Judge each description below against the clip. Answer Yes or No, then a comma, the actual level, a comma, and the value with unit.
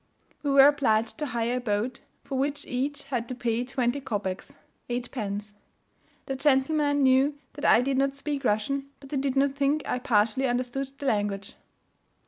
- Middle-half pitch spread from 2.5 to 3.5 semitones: Yes, average, 3.0 semitones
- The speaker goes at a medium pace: Yes, average, 170 wpm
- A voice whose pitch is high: Yes, very high, 265 Hz